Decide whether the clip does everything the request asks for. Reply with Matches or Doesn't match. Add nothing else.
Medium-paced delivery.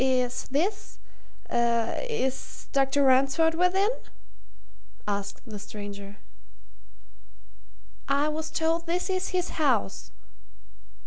Doesn't match